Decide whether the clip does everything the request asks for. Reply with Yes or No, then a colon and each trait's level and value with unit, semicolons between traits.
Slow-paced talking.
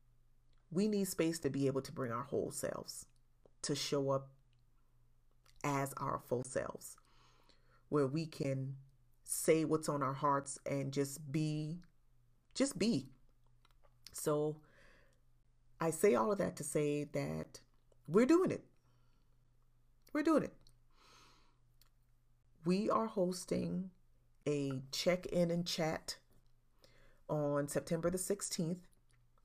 Yes: slow, 120 wpm